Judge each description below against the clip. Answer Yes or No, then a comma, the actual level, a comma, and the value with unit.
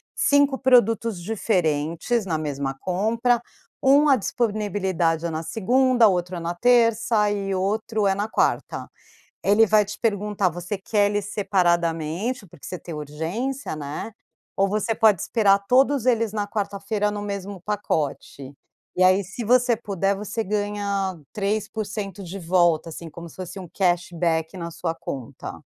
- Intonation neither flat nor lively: Yes, average, 4.0 semitones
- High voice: Yes, high, 200 Hz